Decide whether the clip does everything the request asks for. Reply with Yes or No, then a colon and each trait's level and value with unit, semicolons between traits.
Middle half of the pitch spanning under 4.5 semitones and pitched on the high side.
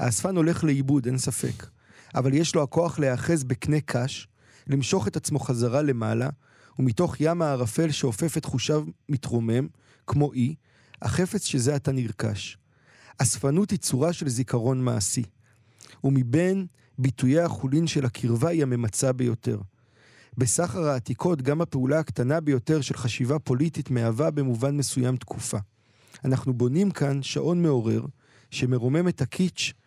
No: average, 3.8 semitones; low, 135 Hz